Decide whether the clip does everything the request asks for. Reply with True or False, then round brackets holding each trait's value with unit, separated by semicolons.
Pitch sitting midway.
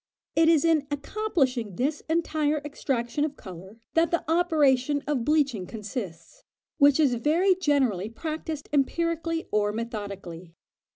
False (285 Hz)